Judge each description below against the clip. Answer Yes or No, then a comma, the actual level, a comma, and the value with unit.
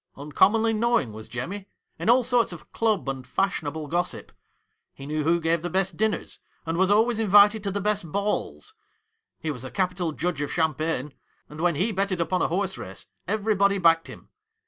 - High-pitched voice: No, medium, 180 Hz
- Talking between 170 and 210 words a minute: Yes, average, 185 wpm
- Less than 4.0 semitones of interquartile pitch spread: No, average, 4.6 semitones